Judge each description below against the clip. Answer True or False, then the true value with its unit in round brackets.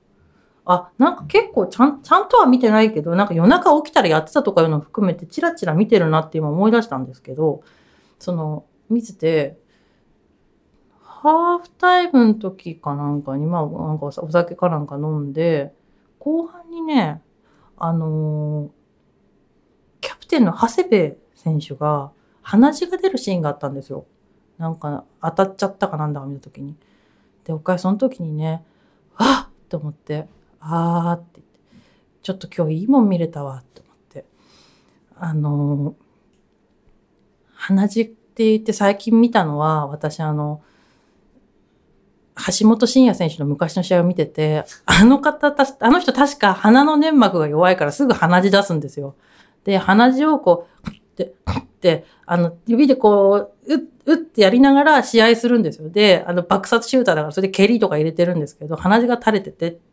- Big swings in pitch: True (7.1 semitones)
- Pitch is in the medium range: True (180 Hz)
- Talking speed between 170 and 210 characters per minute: False (320 characters per minute)